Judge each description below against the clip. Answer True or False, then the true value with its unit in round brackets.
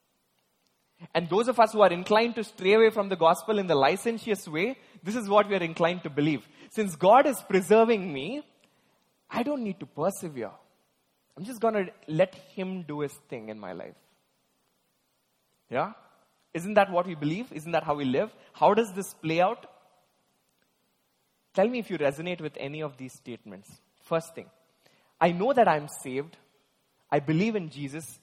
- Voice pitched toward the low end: False (185 Hz)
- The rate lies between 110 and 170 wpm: False (180 wpm)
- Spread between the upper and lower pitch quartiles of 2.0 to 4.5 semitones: False (5.3 semitones)